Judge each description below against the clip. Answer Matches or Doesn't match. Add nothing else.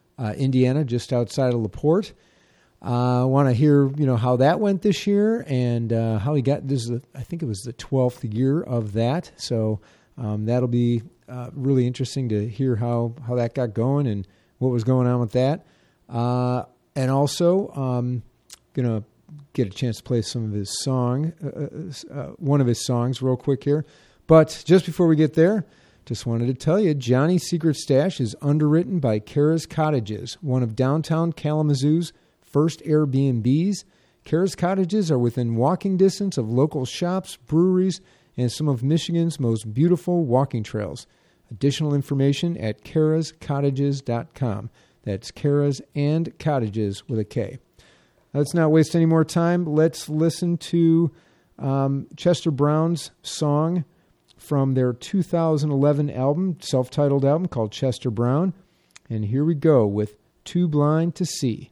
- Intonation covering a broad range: Doesn't match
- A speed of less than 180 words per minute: Matches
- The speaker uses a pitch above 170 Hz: Doesn't match